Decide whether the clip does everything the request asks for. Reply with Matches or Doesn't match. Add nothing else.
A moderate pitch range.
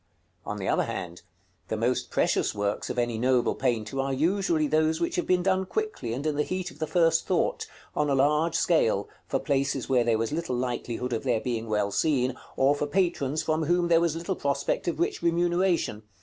Doesn't match